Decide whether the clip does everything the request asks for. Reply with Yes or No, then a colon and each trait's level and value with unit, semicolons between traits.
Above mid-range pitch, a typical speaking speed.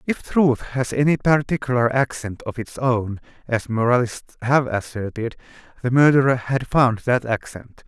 No: low, 125 Hz; average, 145 wpm